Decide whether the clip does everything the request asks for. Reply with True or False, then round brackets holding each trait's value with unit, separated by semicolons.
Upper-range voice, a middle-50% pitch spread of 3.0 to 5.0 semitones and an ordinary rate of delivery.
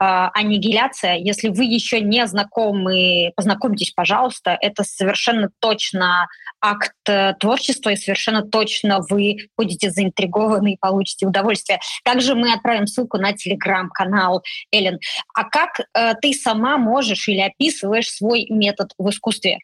False (205 Hz; 2.6 semitones; 130 wpm)